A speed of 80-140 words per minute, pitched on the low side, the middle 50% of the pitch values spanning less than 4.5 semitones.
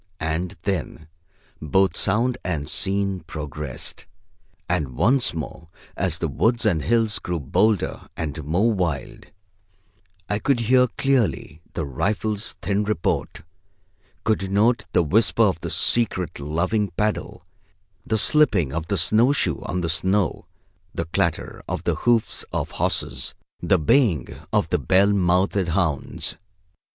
No: slow, 135 wpm; very low, 95 Hz; average, 5.2 semitones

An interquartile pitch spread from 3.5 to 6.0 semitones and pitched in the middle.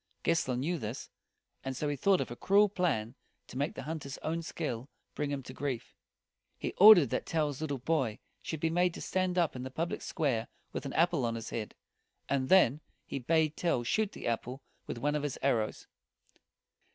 Yes: average, 4.6 semitones; medium, 145 Hz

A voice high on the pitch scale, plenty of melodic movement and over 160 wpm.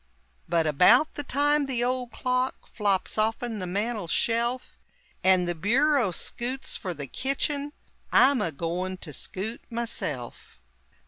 No: high, 230 Hz; wide, 5.9 semitones; slow, 135 wpm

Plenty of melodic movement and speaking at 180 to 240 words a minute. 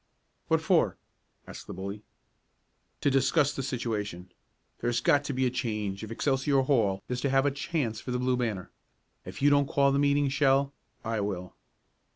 No: average, 4.4 semitones; average, 185 wpm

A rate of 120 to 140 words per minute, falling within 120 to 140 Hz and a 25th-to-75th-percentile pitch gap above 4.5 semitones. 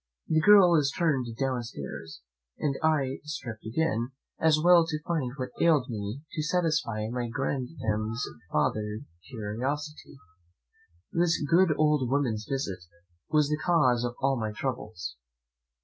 Yes: slow, 135 wpm; low, 135 Hz; average, 5.3 semitones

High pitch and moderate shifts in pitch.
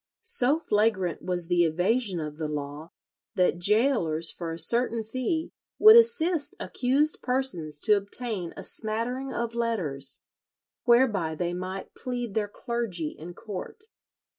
No: high, 210 Hz; wide, 6.5 semitones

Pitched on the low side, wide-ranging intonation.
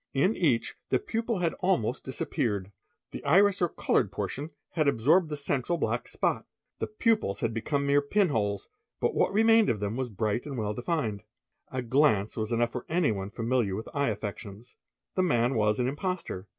Yes: low, 130 Hz; wide, 7.3 semitones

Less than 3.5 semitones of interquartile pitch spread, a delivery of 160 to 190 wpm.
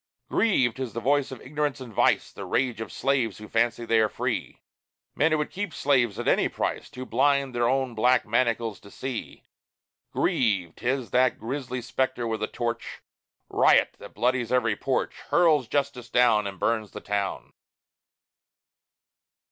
Yes: average, 2.8 semitones; average, 165 wpm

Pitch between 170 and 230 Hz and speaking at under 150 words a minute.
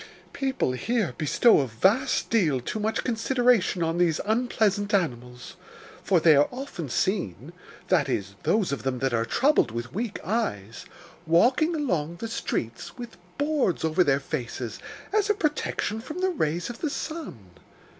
No: medium, 185 Hz; average, 155 wpm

